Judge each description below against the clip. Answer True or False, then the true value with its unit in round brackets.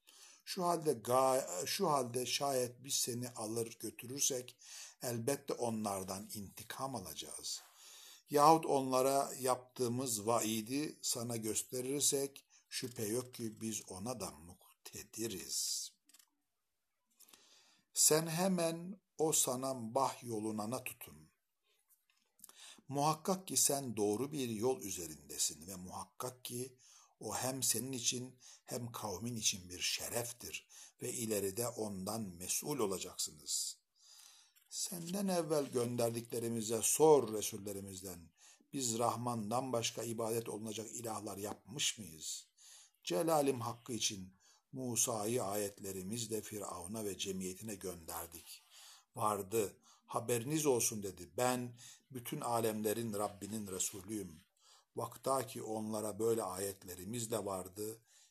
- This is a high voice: False (115 Hz)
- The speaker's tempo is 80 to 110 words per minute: True (100 wpm)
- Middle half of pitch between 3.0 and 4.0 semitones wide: True (3.5 semitones)